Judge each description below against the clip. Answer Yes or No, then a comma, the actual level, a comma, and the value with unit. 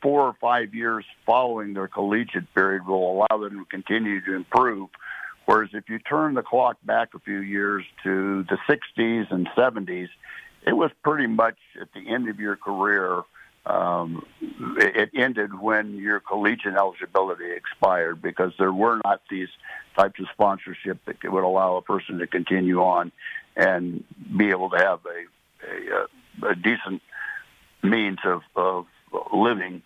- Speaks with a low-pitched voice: Yes, low, 105 Hz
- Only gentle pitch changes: No, average, 4.2 semitones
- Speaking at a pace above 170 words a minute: No, average, 155 wpm